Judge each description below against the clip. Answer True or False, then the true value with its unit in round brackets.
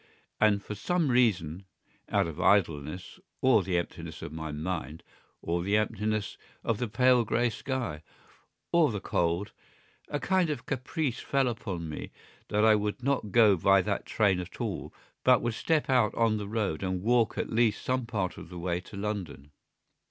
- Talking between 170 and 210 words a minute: True (175 wpm)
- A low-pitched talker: True (105 Hz)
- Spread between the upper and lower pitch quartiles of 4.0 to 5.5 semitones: True (5.0 semitones)